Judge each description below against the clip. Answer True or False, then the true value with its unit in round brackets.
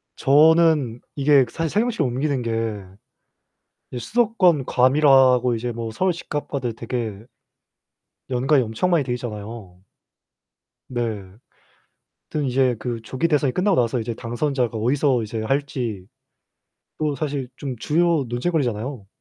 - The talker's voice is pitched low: True (130 Hz)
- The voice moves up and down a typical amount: True (4.2 semitones)